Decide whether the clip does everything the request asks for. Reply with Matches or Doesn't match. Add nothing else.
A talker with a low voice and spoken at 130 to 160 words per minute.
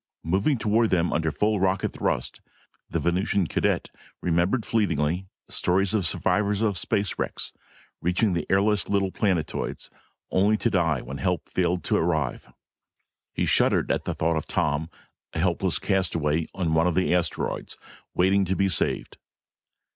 Matches